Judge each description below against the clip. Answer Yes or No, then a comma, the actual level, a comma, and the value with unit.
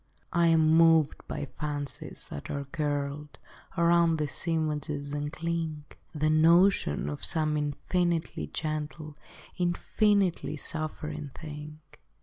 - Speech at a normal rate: No, slow, 110 wpm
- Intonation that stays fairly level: Yes, narrow, 2.0 semitones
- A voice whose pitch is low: No, medium, 155 Hz